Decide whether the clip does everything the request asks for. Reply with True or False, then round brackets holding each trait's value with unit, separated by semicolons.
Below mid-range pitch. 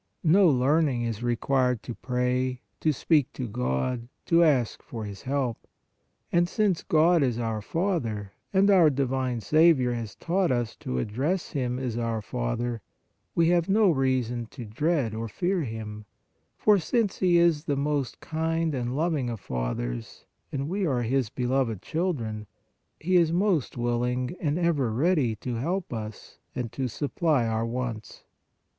True (130 Hz)